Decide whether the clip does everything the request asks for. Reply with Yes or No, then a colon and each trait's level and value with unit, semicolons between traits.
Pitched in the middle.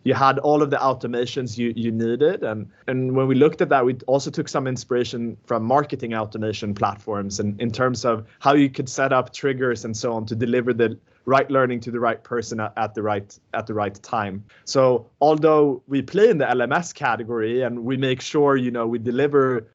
No: low, 125 Hz